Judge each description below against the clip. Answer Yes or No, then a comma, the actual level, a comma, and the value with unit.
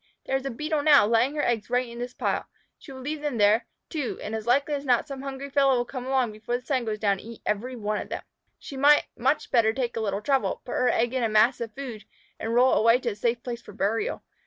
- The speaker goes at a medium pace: No, fast, 275 wpm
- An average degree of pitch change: Yes, average, 3.3 semitones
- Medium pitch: No, high, 245 Hz